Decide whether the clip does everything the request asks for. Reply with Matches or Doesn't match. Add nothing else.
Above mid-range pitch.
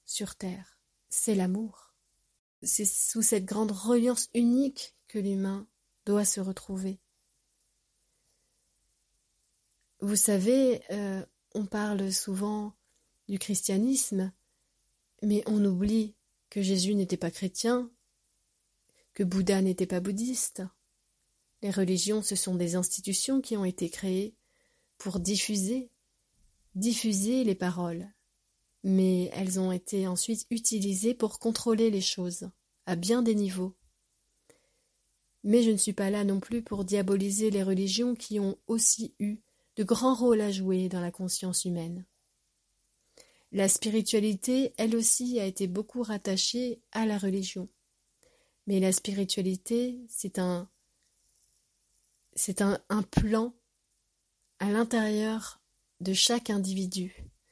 Matches